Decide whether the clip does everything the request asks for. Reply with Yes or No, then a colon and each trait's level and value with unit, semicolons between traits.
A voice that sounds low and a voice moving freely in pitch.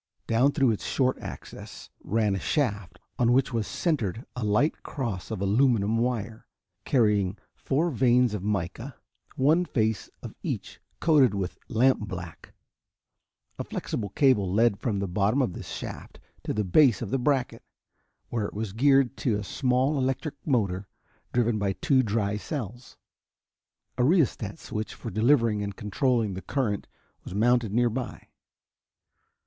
No: low, 115 Hz; average, 4.1 semitones